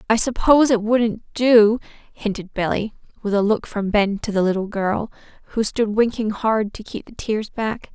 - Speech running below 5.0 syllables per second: Yes, 4.7 syllables/s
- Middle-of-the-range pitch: No, high, 215 Hz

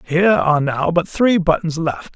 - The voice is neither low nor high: Yes, medium, 170 Hz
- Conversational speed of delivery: Yes, average, 195 wpm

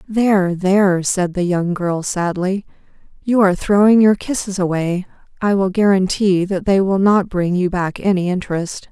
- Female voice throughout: Yes, female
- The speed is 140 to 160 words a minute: No, average, 170 wpm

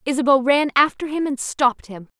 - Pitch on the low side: No, very high, 270 Hz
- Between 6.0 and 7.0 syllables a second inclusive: No, 5.7 syllables/s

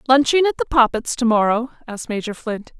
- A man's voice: No, female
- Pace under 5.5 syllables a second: No, 6.4 syllables/s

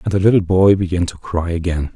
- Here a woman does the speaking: No, male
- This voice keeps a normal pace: No, fast, 245 wpm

